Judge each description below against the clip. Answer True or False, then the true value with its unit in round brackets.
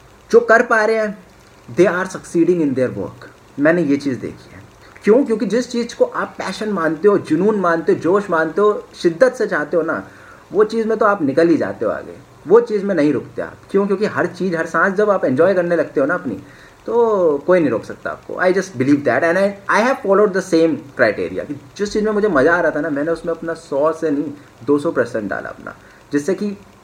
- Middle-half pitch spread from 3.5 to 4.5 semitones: False (5.0 semitones)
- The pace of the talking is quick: True (235 wpm)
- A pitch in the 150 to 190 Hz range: True (185 Hz)